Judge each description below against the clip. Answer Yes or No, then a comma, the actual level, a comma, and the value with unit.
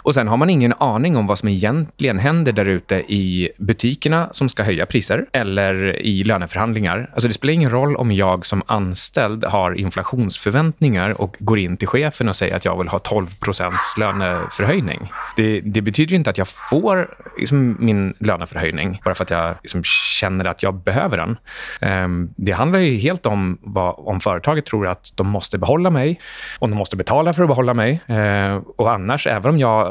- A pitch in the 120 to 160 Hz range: No, low, 105 Hz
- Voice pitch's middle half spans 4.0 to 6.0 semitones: Yes, wide, 5.4 semitones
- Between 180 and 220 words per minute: Yes, fast, 195 wpm